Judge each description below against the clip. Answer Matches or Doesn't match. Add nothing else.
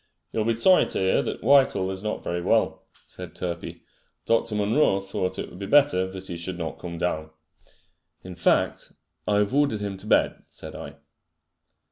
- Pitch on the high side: Doesn't match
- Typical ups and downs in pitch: Matches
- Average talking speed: Matches